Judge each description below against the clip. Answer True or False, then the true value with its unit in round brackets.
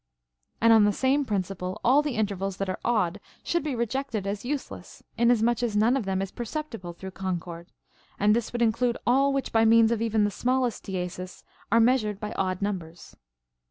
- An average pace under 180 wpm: False (195 wpm)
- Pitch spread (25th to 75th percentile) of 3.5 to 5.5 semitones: True (3.9 semitones)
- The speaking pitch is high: True (220 Hz)